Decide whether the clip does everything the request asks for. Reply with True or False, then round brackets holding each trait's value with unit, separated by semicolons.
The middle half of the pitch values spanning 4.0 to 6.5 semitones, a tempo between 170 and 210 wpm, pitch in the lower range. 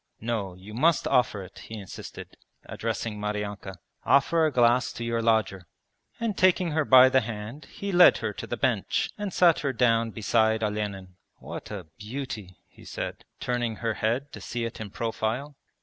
True (4.3 semitones; 175 wpm; 115 Hz)